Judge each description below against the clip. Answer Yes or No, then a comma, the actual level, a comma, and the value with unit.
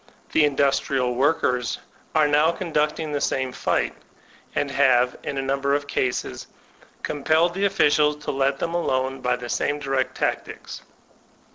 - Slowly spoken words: No, average, 150 wpm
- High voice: No, medium, 140 Hz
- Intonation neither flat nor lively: No, narrow, 2.3 semitones